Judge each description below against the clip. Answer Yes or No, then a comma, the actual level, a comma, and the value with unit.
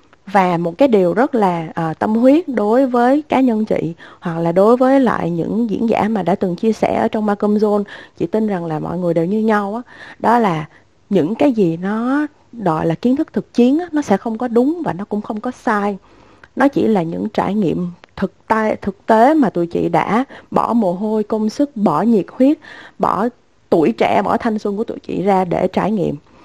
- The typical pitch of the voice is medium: No, high, 215 Hz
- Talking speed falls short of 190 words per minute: No, average, 225 wpm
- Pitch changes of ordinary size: Yes, average, 4.2 semitones